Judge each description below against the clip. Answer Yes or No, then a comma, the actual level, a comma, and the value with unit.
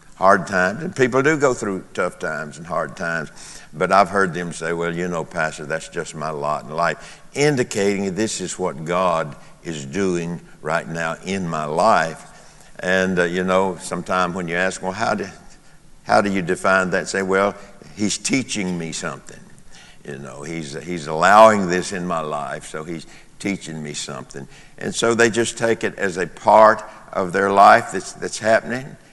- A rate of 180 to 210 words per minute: Yes, average, 185 wpm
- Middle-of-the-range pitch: No, very low, 95 Hz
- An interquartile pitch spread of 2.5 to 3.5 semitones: Yes, average, 2.8 semitones